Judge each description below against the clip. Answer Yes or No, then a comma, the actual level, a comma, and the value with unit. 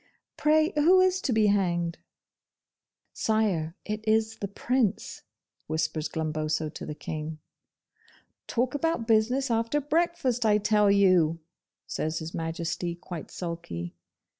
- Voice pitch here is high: Yes, high, 205 Hz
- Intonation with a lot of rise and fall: Yes, wide, 7.0 semitones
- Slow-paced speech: Yes, slow, 120 wpm